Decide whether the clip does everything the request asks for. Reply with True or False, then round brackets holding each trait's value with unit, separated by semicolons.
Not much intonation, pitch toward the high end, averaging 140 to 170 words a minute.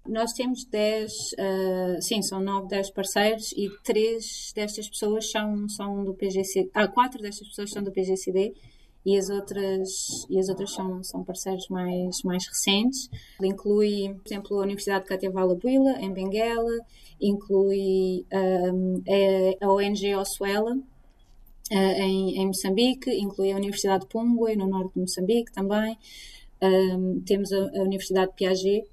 True (1.8 semitones; 195 Hz; 150 wpm)